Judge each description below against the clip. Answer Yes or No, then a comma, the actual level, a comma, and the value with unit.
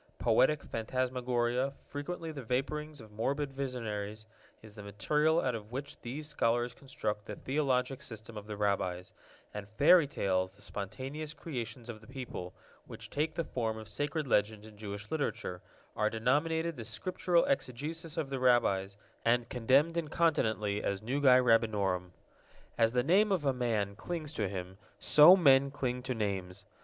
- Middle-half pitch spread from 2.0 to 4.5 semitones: No, wide, 5.4 semitones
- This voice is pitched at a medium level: No, low, 125 Hz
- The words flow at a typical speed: Yes, average, 155 wpm